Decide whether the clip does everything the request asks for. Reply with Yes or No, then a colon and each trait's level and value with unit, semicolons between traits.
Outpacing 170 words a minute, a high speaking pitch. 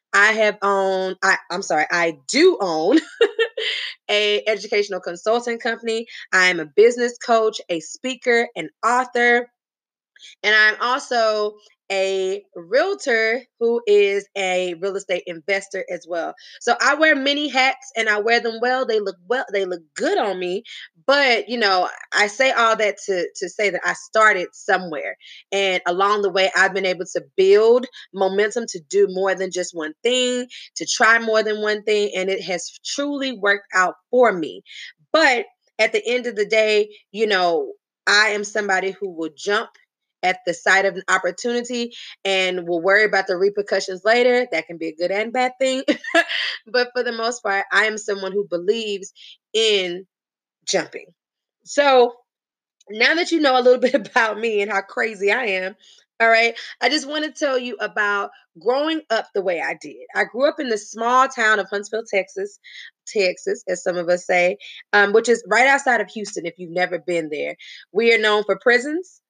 Yes: average, 180 wpm; high, 215 Hz